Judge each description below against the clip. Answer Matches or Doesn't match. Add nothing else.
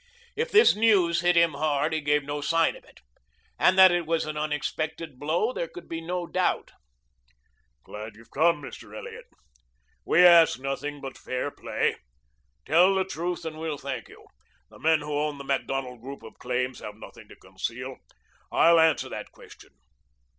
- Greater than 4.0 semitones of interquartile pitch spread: Doesn't match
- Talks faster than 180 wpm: Doesn't match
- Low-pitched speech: Doesn't match